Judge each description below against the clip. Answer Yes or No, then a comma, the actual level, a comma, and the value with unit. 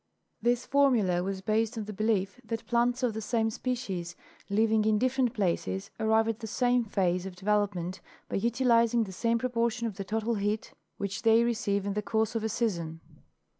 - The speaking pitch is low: No, high, 220 Hz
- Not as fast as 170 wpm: No, average, 185 wpm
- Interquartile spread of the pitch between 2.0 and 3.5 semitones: Yes, average, 2.9 semitones